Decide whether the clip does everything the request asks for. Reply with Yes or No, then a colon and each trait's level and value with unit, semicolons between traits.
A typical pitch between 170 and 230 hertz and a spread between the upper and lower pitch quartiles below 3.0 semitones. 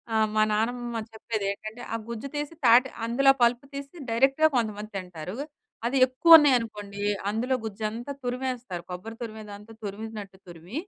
No: high, 225 Hz; average, 3.3 semitones